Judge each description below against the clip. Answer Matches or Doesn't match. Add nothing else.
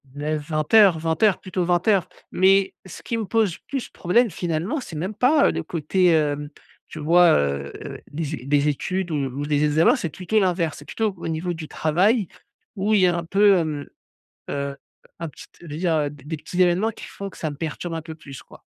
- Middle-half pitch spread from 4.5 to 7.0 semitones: Doesn't match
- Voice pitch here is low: Doesn't match